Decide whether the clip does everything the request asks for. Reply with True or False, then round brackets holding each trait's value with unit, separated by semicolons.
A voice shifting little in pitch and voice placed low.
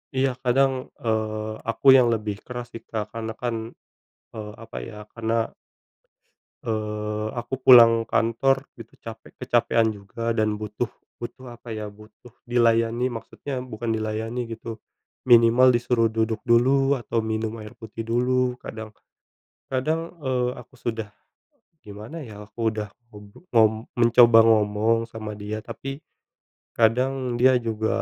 True (1.9 semitones; 115 Hz)